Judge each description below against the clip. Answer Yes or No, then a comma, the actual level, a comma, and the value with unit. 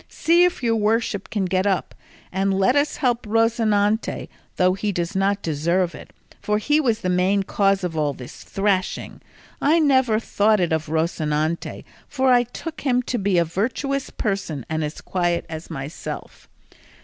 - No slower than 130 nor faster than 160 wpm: No, average, 170 wpm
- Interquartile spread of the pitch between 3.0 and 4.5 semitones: No, average, 5.1 semitones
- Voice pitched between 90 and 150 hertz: No, high, 200 Hz